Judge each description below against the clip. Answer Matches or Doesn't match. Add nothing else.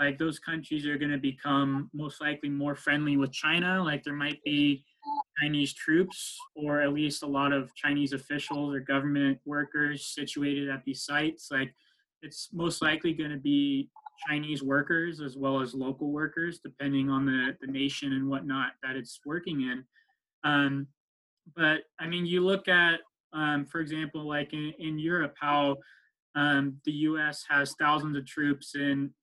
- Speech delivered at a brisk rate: Doesn't match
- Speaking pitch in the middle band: Matches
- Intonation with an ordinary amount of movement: Doesn't match